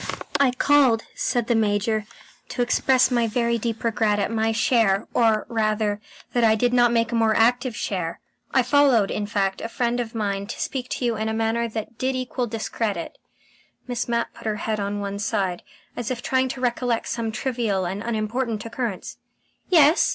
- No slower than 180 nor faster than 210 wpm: Yes, average, 195 wpm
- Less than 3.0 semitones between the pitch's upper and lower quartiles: Yes, narrow, 2.4 semitones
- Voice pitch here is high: Yes, high, 230 Hz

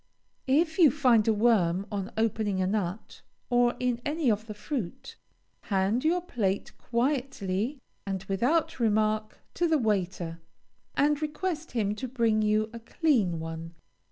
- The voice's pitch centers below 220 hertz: No, high, 225 Hz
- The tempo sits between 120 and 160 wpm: Yes, average, 145 wpm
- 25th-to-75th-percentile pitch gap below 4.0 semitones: No, average, 5.3 semitones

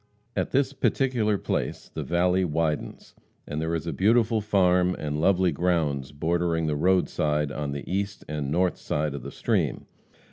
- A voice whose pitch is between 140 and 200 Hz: No, very low, 85 Hz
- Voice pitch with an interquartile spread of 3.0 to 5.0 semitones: Yes, average, 3.9 semitones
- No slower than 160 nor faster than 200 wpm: Yes, average, 165 wpm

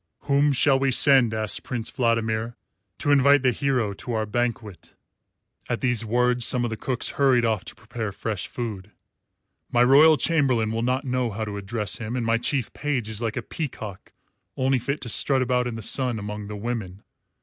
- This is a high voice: No, low, 120 Hz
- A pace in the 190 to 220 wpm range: Yes, average, 195 wpm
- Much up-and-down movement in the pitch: No, average, 3.1 semitones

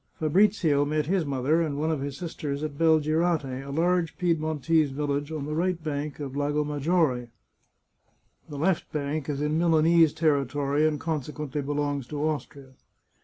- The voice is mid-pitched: Yes, medium, 150 Hz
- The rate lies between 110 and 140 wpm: No, average, 165 wpm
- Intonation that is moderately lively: No, narrow, 2.1 semitones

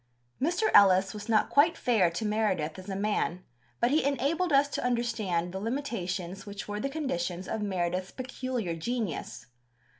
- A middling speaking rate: Yes, average, 160 wpm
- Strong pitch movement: Yes, wide, 5.7 semitones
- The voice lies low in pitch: No, high, 210 Hz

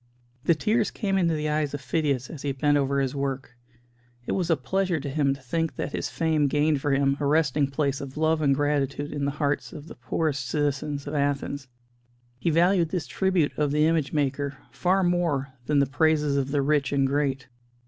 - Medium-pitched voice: Yes, medium, 145 Hz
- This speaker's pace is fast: Yes, fast, 210 wpm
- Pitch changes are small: Yes, narrow, 2.3 semitones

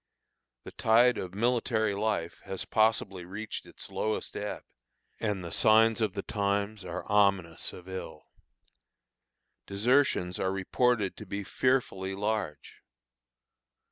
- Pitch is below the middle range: Yes, low, 100 Hz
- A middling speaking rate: No, slow, 120 wpm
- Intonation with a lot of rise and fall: No, narrow, 2.6 semitones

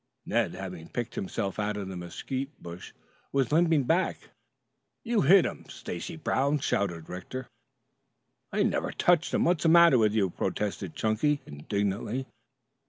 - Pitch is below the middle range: Yes, low, 110 Hz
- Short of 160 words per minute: Yes, average, 145 wpm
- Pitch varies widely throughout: Yes, wide, 7.8 semitones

